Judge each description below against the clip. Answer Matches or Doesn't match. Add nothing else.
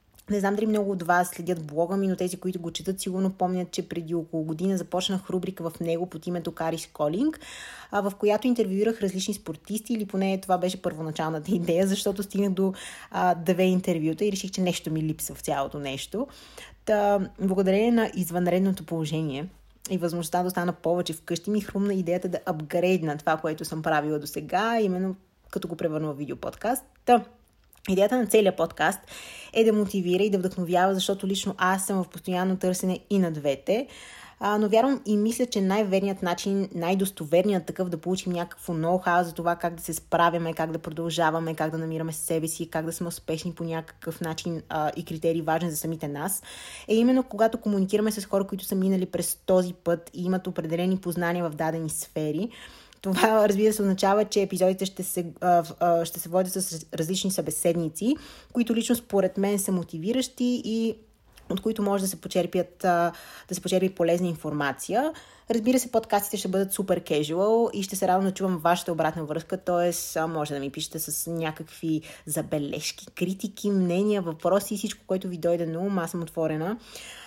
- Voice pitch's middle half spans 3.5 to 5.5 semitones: Doesn't match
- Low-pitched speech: Doesn't match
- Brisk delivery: Matches